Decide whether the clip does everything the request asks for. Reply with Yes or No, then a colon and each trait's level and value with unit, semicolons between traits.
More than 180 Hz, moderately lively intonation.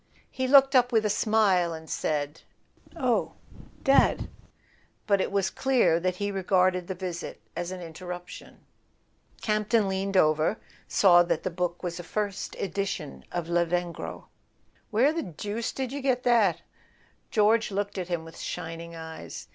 Yes: high, 190 Hz; average, 3.8 semitones